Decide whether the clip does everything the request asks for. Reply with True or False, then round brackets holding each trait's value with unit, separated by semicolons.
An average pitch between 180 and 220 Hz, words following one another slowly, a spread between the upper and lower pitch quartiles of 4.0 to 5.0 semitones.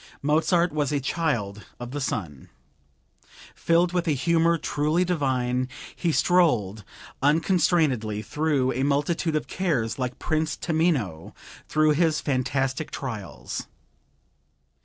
False (145 Hz; 115 wpm; 4.6 semitones)